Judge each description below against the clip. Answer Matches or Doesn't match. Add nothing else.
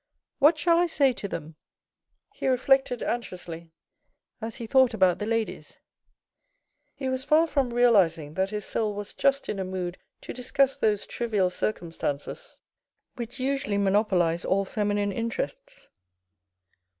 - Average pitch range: Doesn't match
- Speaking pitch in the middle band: Doesn't match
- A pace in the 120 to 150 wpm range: Matches